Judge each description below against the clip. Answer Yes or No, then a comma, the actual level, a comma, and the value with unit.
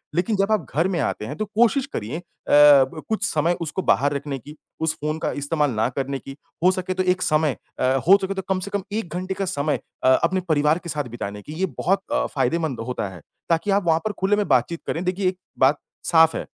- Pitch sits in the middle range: Yes, medium, 165 Hz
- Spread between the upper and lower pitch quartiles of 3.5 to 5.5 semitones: Yes, average, 4.6 semitones